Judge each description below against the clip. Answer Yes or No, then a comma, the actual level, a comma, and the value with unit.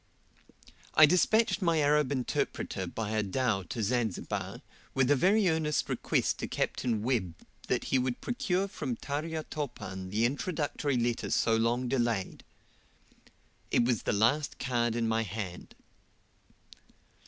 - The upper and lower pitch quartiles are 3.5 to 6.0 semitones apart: Yes, average, 5.1 semitones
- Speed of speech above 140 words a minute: No, slow, 135 wpm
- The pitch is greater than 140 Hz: No, low, 125 Hz